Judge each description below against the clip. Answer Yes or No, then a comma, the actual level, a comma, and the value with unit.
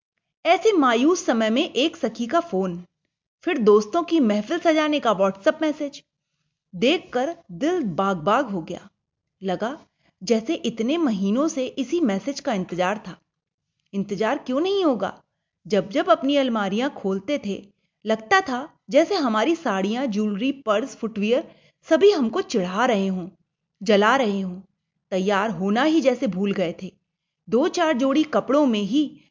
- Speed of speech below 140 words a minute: No, average, 145 wpm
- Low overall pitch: No, high, 225 Hz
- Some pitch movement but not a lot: No, wide, 7.2 semitones